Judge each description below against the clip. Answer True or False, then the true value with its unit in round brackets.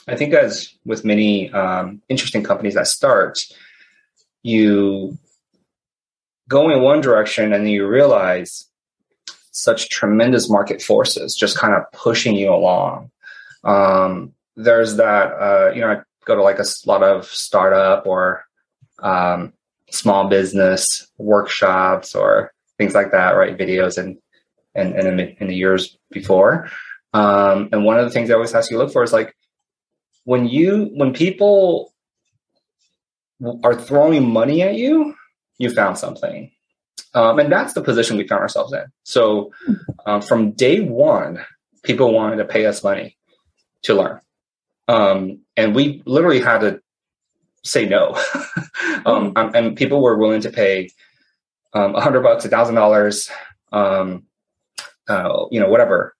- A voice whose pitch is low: True (115 Hz)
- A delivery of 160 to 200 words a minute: False (145 wpm)